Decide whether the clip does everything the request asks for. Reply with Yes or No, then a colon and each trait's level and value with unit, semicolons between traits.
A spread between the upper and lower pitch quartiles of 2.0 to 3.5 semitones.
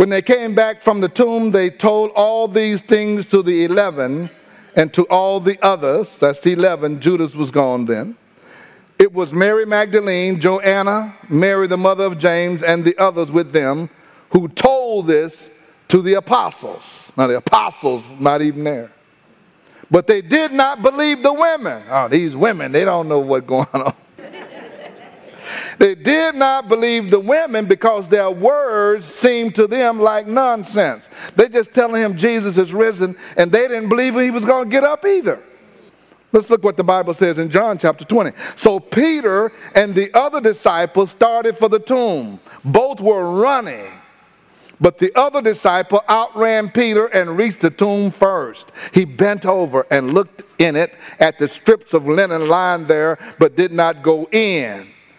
No: average, 4.8 semitones